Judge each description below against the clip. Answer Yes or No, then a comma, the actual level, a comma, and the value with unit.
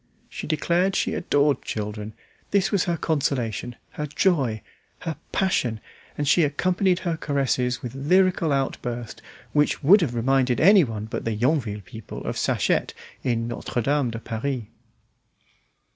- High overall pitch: No, medium, 140 Hz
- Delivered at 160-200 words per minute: No, average, 140 wpm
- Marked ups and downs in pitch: Yes, wide, 6.0 semitones